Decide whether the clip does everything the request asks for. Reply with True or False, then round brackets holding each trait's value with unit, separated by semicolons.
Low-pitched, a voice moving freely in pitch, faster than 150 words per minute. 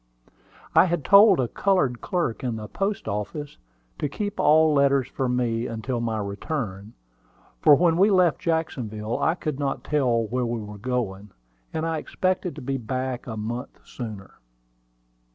True (130 Hz; 5.9 semitones; 160 wpm)